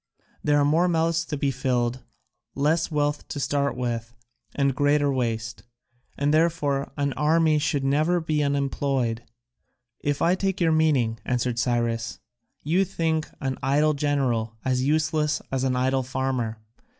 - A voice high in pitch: No, medium, 140 Hz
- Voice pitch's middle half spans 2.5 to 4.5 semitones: Yes, average, 3.3 semitones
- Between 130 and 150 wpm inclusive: Yes, average, 145 wpm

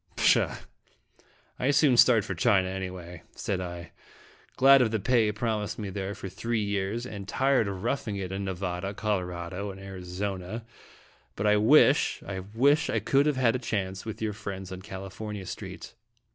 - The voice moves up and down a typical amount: Yes, average, 3.3 semitones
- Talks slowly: No, average, 175 wpm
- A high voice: No, low, 100 Hz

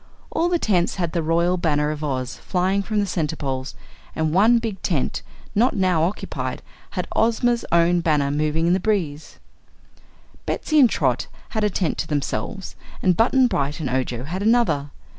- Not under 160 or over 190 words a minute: Yes, average, 170 wpm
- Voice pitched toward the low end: No, medium, 175 Hz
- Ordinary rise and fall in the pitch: No, wide, 5.8 semitones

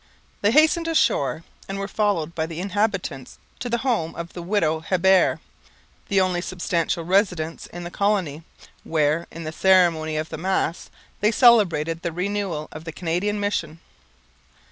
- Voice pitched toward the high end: No, medium, 175 Hz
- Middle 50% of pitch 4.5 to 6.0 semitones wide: No, average, 3.9 semitones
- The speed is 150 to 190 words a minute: Yes, average, 155 wpm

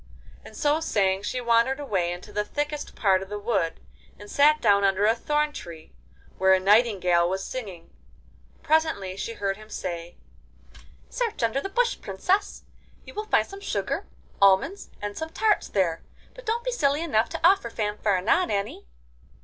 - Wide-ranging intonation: Yes, wide, 7.8 semitones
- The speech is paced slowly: No, average, 165 wpm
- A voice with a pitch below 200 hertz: No, high, 220 Hz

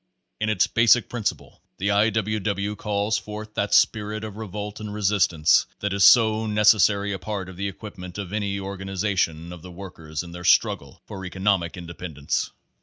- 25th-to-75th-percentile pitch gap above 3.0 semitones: No, narrow, 2.6 semitones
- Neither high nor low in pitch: No, low, 100 Hz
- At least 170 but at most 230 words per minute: Yes, average, 180 wpm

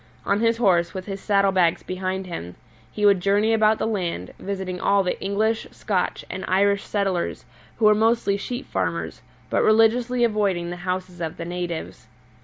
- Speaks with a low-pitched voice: No, high, 195 Hz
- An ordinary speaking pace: Yes, average, 175 wpm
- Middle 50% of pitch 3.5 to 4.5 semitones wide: No, average, 3.0 semitones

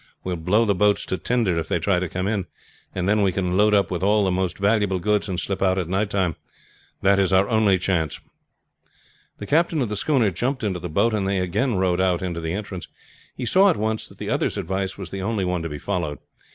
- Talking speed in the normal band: No, fast, 245 wpm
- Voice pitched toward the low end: Yes, very low, 95 Hz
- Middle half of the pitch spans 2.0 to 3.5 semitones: Yes, average, 2.7 semitones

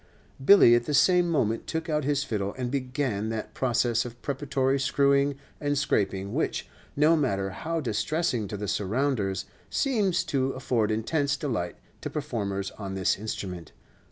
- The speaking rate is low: No, average, 155 wpm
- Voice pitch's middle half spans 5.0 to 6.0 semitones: Yes, wide, 5.6 semitones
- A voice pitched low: Yes, low, 130 Hz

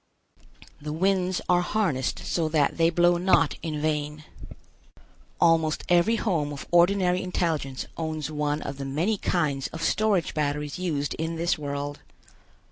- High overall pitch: No, medium, 160 Hz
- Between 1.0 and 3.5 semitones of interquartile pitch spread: Yes, average, 3.1 semitones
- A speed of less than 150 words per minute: Yes, average, 140 wpm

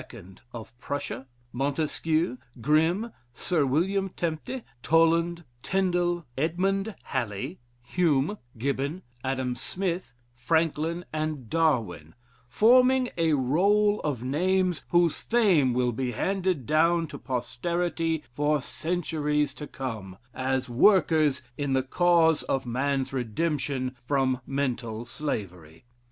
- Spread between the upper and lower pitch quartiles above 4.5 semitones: Yes, average, 5.0 semitones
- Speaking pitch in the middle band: Yes, medium, 150 Hz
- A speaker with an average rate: No, slow, 105 wpm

